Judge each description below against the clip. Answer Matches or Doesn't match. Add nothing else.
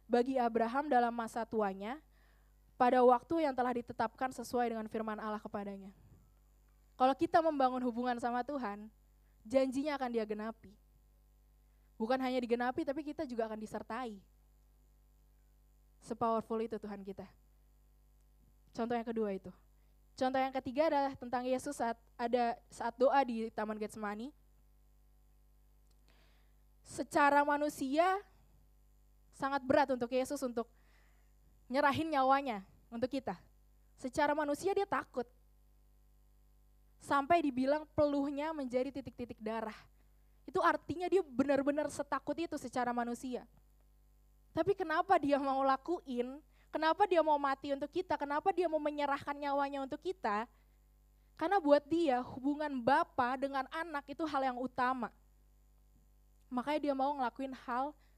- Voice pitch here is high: Matches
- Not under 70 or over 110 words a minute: Doesn't match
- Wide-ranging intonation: Doesn't match